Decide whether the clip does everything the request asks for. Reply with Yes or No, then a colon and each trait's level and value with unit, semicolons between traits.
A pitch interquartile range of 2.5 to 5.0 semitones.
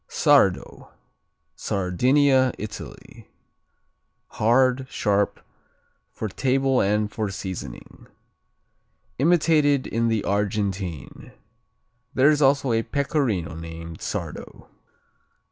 No: wide, 5.5 semitones